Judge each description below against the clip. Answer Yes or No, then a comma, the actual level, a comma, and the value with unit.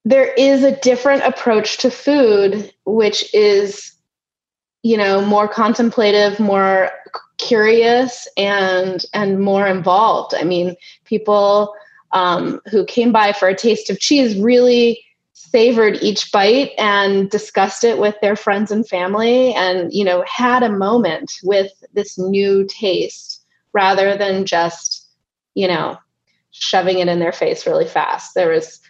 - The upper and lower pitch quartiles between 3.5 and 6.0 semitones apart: Yes, average, 4.0 semitones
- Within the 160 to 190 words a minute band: No, average, 140 wpm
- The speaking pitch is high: Yes, high, 210 Hz